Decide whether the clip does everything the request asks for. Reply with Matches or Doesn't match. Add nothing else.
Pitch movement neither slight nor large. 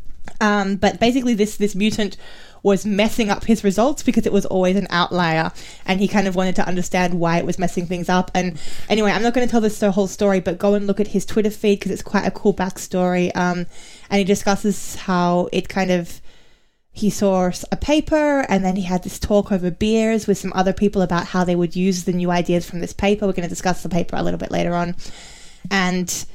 Doesn't match